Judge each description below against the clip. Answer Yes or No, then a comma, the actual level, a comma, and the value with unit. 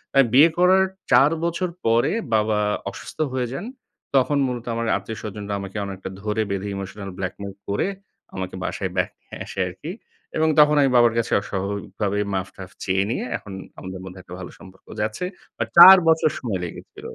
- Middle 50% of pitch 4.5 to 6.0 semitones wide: Yes, wide, 5.5 semitones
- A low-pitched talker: Yes, low, 105 Hz